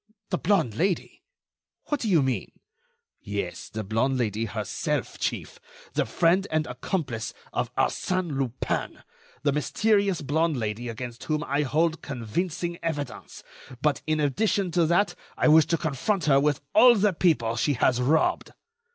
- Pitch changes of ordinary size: No, wide, 5.8 semitones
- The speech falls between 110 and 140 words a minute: No, average, 150 wpm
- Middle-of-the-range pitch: Yes, medium, 150 Hz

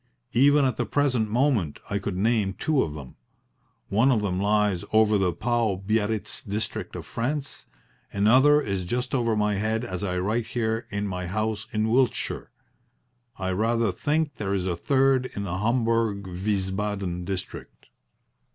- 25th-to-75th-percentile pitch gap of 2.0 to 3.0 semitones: No, average, 3.6 semitones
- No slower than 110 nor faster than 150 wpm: No, average, 160 wpm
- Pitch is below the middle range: Yes, low, 105 Hz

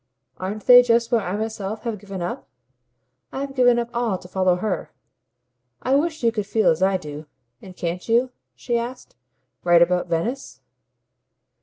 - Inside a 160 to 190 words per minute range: Yes, average, 165 wpm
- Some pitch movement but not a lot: Yes, average, 4.7 semitones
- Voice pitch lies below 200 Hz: No, high, 215 Hz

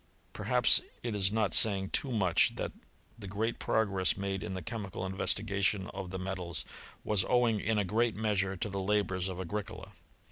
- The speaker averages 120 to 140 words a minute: No, average, 175 wpm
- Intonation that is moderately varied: No, narrow, 2.2 semitones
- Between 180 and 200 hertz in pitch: No, low, 100 Hz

